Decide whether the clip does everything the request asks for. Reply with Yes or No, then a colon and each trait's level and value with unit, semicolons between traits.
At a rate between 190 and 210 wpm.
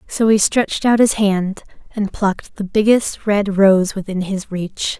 No: average, 180 wpm